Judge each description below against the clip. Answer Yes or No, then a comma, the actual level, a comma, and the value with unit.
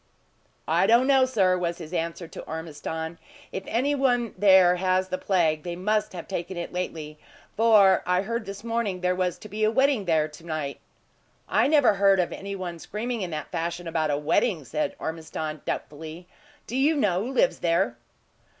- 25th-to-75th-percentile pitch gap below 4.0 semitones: No, average, 4.7 semitones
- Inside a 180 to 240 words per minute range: Yes, average, 185 wpm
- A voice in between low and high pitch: Yes, medium, 180 Hz